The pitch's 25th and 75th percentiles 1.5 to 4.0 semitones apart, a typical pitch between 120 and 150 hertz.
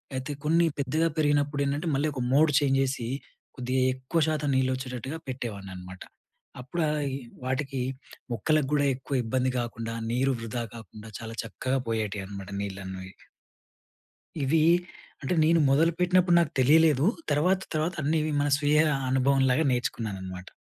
No: average, 4.6 semitones; low, 135 Hz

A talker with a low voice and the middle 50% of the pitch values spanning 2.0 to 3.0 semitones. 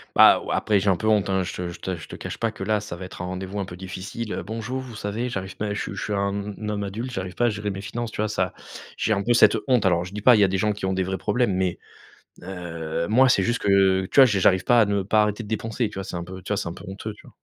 Yes: low, 100 Hz; narrow, 2.5 semitones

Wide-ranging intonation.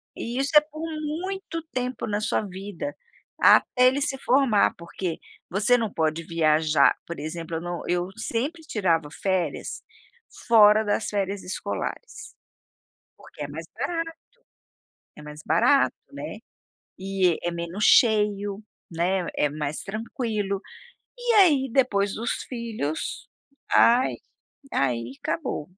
Yes: wide, 6.8 semitones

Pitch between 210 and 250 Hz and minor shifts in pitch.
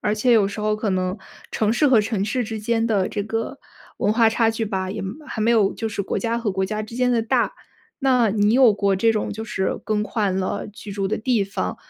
Yes: high, 215 Hz; narrow, 2.3 semitones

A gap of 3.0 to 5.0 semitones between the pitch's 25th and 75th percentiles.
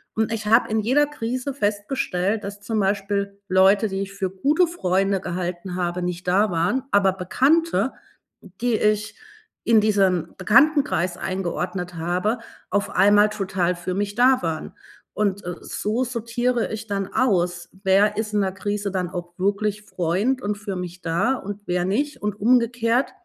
Yes: average, 3.4 semitones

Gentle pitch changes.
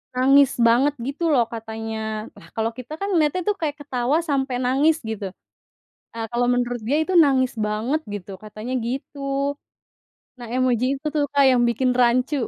No: average, 3.2 semitones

